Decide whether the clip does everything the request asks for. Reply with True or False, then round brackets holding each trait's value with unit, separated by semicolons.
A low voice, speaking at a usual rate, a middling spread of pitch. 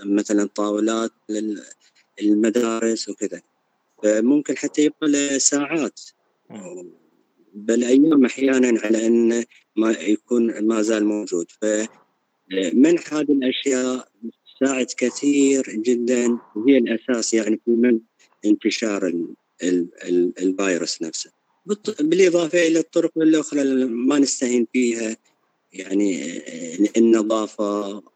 True (120 Hz; 95 wpm; 4.8 semitones)